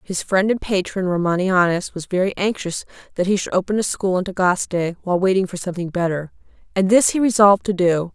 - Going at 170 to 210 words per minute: Yes, average, 200 wpm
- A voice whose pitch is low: No, medium, 185 Hz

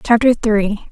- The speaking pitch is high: Yes, high, 220 Hz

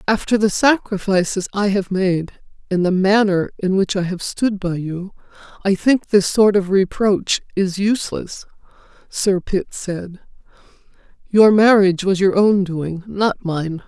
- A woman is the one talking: Yes, female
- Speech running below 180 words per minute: Yes, average, 150 wpm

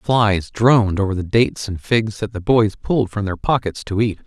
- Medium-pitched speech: No, low, 105 Hz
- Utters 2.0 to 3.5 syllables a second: No, 5.0 syllables/s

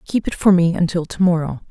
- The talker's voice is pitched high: No, medium, 175 Hz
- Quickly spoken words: Yes, fast, 245 wpm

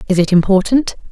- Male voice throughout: No, female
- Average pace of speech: Yes, average, 160 wpm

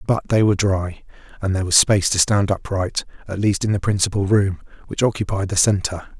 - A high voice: No, low, 100 Hz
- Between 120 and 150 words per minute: No, fast, 205 wpm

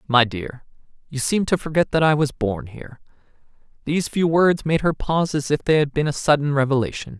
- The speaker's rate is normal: No, fast, 210 wpm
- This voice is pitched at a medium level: Yes, medium, 145 Hz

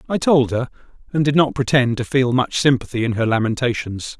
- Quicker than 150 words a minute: Yes, average, 200 wpm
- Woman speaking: No, male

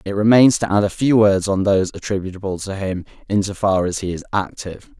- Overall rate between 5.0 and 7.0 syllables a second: Yes, 6.0 syllables/s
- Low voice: Yes, low, 100 Hz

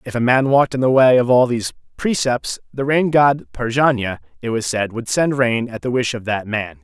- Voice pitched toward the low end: Yes, low, 125 Hz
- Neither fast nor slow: No, fast, 235 wpm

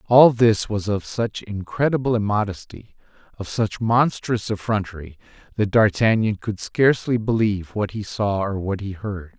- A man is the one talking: Yes, male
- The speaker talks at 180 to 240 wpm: No, average, 145 wpm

